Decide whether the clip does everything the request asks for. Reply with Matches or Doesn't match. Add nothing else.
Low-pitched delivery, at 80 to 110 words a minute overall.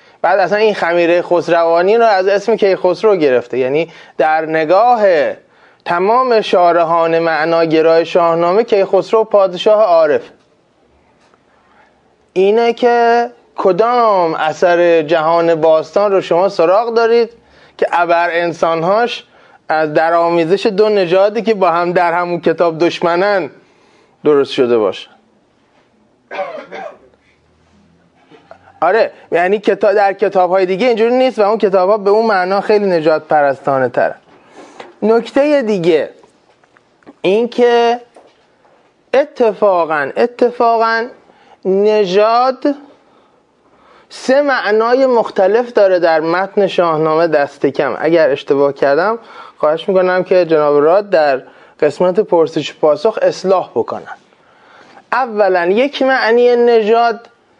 Doesn't match